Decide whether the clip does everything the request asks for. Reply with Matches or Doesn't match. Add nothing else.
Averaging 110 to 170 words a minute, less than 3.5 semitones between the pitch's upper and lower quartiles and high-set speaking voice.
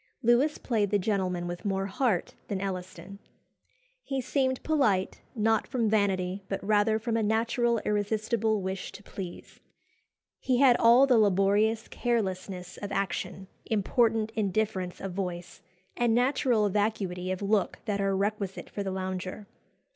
Matches